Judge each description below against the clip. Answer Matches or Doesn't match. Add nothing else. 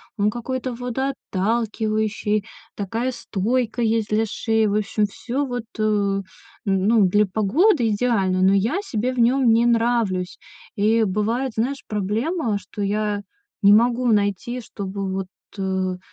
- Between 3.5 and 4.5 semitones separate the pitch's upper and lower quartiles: Doesn't match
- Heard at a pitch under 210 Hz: Doesn't match